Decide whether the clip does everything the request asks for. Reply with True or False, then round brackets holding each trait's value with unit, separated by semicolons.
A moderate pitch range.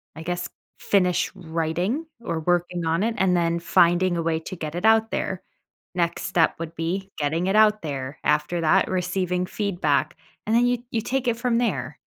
True (3.8 semitones)